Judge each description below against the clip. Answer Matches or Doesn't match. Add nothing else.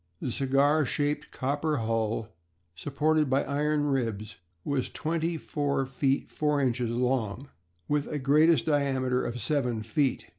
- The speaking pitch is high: Doesn't match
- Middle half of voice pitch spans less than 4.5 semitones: Matches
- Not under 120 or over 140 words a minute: Matches